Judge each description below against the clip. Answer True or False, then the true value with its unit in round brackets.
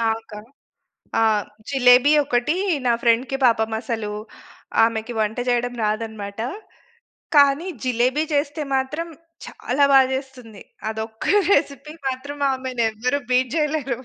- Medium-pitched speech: False (250 Hz)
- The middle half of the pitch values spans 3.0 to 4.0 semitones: True (3.6 semitones)